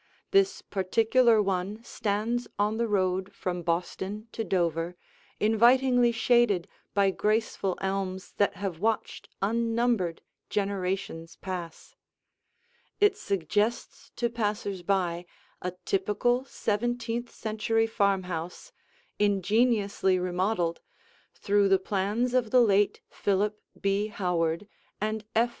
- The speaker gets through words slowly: Yes, slow, 105 wpm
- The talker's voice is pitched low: No, high, 205 Hz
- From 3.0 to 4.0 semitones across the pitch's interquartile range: Yes, average, 3.3 semitones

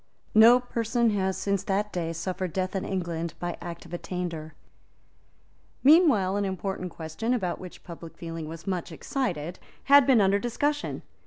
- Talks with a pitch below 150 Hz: No, high, 190 Hz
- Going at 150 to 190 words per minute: Yes, average, 155 wpm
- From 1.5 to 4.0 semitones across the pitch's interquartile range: No, average, 4.6 semitones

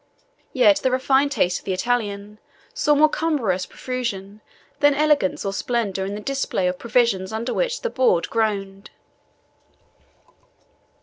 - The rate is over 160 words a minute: No, slow, 135 wpm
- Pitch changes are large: Yes, wide, 6.0 semitones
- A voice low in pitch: No, high, 230 Hz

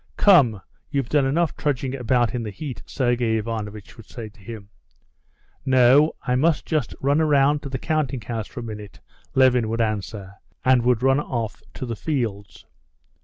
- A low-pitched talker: Yes, low, 125 Hz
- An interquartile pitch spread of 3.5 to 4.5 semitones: Yes, average, 3.8 semitones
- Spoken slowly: No, average, 175 wpm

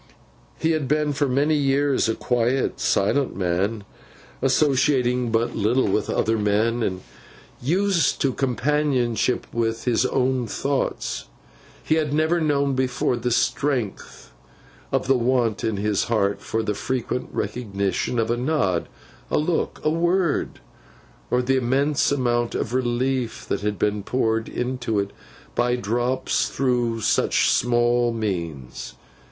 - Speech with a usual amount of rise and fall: Yes, average, 3.5 semitones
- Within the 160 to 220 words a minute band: No, slow, 135 wpm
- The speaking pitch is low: Yes, low, 125 Hz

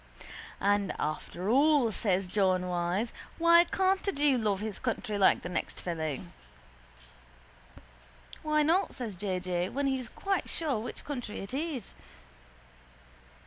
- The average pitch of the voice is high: Yes, high, 220 Hz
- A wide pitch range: Yes, wide, 7.8 semitones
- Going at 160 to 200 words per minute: No, slow, 135 wpm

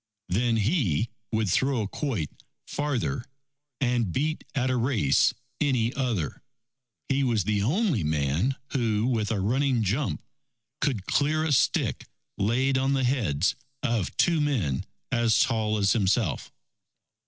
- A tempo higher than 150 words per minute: No, slow, 135 wpm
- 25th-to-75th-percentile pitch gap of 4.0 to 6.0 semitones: Yes, average, 4.7 semitones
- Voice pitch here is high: No, low, 120 Hz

